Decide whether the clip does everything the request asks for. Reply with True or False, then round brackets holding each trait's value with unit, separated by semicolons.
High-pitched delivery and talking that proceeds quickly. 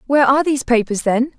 True (260 Hz; 215 wpm)